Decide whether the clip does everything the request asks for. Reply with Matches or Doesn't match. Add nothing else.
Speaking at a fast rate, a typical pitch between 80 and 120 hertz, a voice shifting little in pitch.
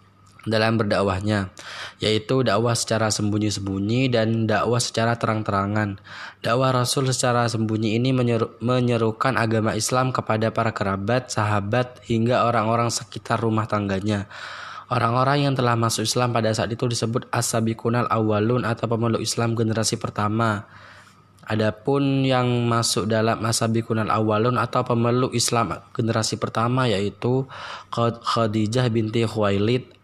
Doesn't match